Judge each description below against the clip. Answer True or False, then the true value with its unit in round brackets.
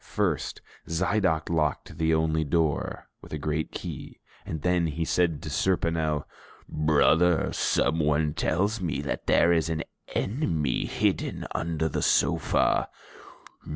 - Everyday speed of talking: False (125 wpm)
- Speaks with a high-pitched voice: False (80 Hz)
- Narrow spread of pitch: True (1.8 semitones)